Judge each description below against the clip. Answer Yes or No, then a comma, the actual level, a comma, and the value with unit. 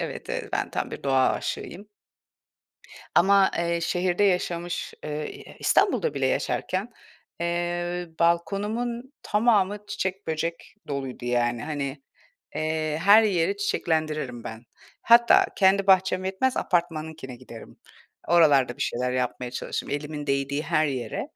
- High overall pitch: No, medium, 170 Hz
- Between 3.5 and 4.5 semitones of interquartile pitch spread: No, average, 5.1 semitones